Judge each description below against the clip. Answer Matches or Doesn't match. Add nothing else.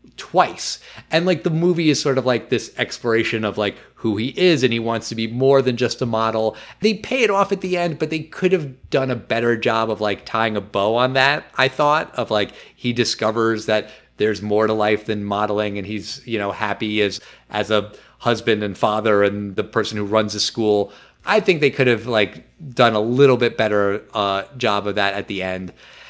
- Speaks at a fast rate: Matches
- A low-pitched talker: Matches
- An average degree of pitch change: Matches